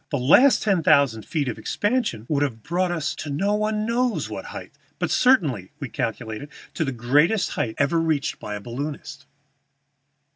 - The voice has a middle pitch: Yes, medium, 150 Hz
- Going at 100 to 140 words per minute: No, average, 175 wpm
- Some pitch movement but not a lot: No, wide, 7.9 semitones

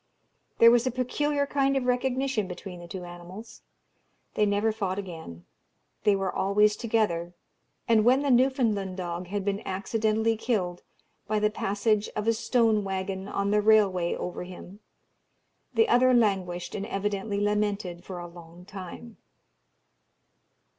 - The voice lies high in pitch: Yes, high, 205 Hz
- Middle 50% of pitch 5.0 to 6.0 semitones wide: No, average, 3.5 semitones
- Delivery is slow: No, average, 145 wpm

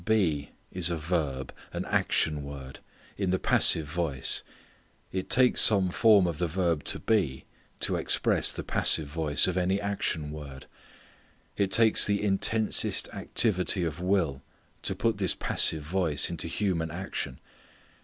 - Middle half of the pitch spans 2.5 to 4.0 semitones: No, average, 4.4 semitones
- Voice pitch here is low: Yes, very low, 85 Hz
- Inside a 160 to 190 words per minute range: No, average, 145 wpm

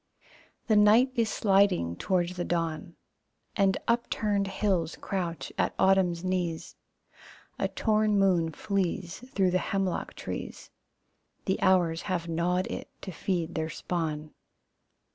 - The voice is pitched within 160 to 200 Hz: Yes, medium, 185 Hz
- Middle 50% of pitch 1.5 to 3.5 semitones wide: Yes, average, 2.8 semitones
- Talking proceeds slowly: Yes, slow, 125 wpm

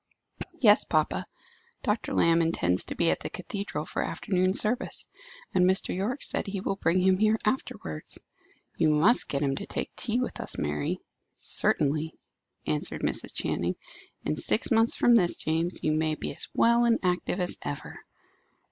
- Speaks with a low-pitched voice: No, medium, 180 Hz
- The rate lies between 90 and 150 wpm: No, average, 165 wpm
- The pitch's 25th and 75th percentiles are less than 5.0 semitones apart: No, wide, 5.6 semitones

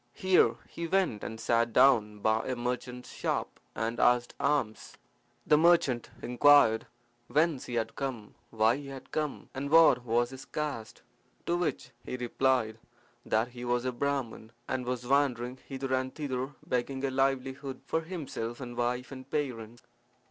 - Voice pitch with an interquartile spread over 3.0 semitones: No, average, 2.7 semitones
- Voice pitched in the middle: No, low, 125 Hz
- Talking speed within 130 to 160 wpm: Yes, average, 155 wpm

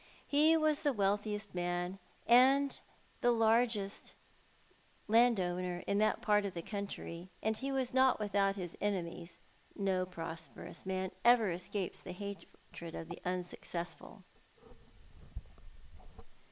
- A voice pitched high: Yes, high, 200 Hz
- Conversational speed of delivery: No, slow, 115 wpm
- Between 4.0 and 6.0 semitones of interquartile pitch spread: Yes, average, 4.3 semitones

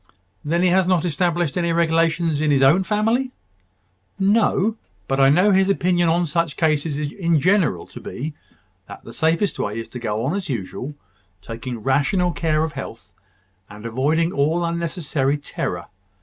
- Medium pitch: Yes, medium, 165 Hz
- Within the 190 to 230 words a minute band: No, average, 165 wpm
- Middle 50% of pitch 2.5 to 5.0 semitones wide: Yes, average, 4.2 semitones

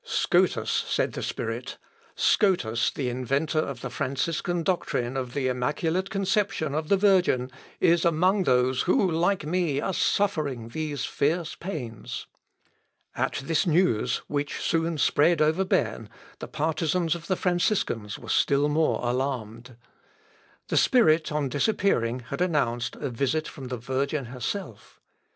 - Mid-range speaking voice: Yes, medium, 150 Hz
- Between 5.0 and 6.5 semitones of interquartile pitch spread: Yes, wide, 5.4 semitones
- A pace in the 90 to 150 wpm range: Yes, slow, 135 wpm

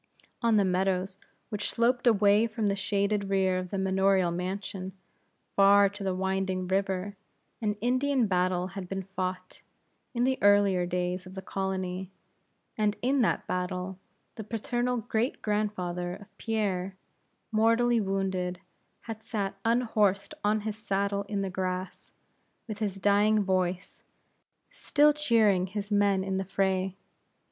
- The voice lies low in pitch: No, high, 195 Hz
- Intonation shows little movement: Yes, narrow, 2.3 semitones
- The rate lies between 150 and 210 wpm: No, average, 140 wpm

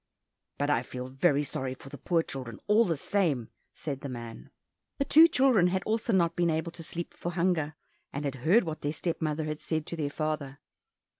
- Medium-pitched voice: Yes, medium, 155 Hz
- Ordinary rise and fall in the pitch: Yes, average, 4.0 semitones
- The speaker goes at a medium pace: No, fast, 210 wpm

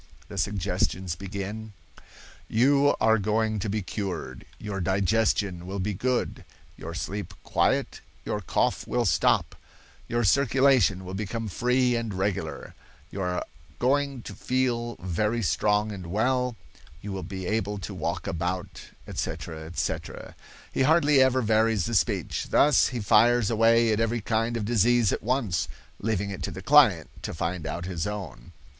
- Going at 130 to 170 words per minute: Yes, average, 150 wpm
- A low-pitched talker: Yes, low, 105 Hz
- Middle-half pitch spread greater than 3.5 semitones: Yes, average, 3.9 semitones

